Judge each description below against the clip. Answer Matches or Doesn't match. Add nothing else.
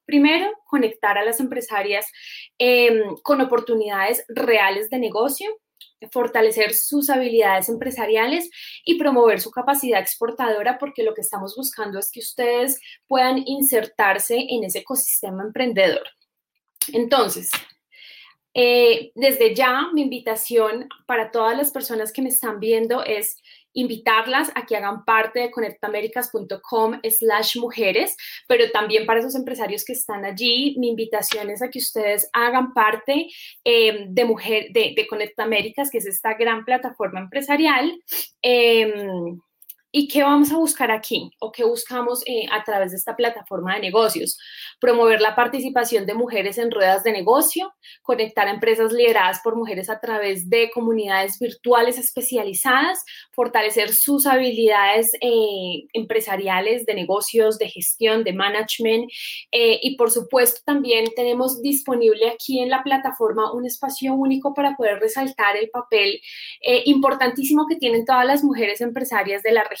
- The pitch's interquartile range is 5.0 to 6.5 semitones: Doesn't match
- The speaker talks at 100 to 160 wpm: Matches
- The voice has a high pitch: Matches